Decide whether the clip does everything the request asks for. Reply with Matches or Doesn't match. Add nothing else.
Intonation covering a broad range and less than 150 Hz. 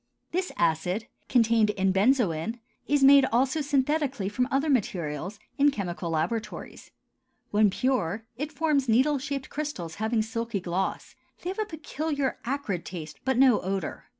Doesn't match